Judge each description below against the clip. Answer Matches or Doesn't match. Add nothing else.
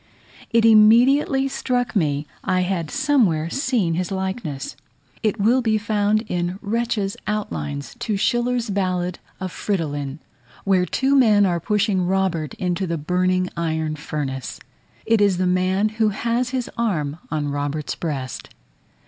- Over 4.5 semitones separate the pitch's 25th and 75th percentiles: Matches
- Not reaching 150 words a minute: Matches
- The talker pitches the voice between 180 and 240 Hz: Matches